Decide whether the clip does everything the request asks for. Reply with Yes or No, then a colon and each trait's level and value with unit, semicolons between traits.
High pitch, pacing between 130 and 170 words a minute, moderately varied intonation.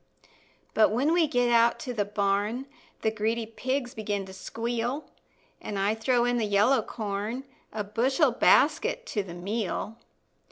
Yes: high, 230 Hz; average, 155 wpm; average, 3.4 semitones